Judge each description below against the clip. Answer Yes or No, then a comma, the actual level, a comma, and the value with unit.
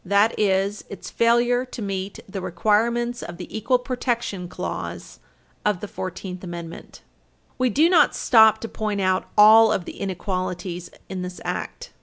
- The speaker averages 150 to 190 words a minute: Yes, average, 155 wpm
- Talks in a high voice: Yes, high, 205 Hz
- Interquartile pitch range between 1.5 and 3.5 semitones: No, average, 3.9 semitones